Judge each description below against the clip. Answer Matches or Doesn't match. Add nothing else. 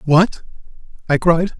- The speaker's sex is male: Matches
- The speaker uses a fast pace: Doesn't match